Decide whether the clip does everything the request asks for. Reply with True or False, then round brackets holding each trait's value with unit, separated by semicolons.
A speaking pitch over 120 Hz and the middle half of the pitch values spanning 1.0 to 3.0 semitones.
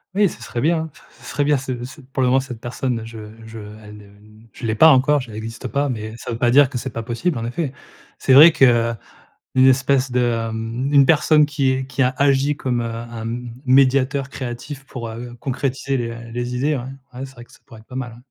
True (130 Hz; 2.7 semitones)